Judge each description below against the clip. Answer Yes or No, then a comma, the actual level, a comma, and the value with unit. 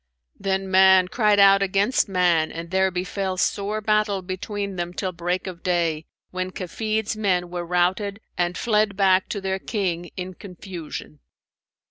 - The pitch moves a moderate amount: No, narrow, 2.1 semitones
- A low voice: No, high, 190 Hz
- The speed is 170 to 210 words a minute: No, average, 150 wpm